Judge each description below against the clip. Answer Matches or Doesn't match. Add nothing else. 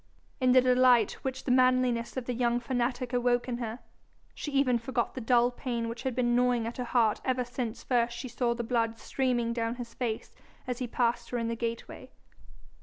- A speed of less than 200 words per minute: Doesn't match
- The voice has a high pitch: Matches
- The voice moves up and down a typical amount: Doesn't match